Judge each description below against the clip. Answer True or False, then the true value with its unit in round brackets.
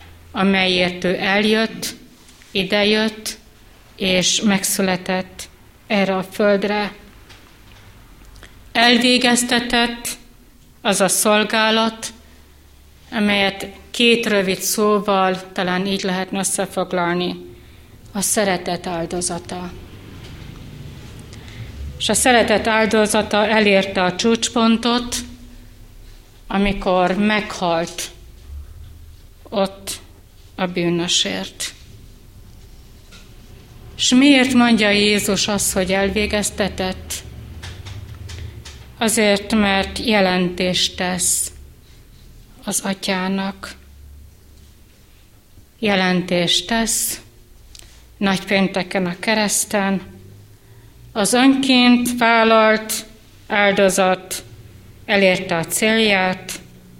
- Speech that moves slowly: True (65 wpm)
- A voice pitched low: False (190 Hz)